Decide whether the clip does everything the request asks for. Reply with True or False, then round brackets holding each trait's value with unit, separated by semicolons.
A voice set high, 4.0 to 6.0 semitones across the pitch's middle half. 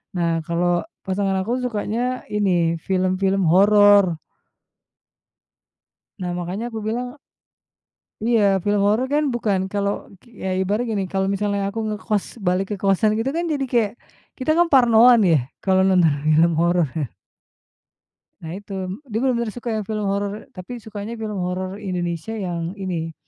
False (200 Hz; 3.3 semitones)